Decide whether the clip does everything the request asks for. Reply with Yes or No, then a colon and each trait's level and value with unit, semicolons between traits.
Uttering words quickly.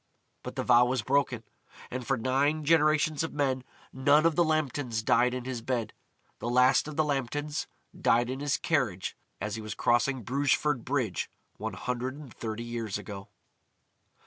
No: average, 170 wpm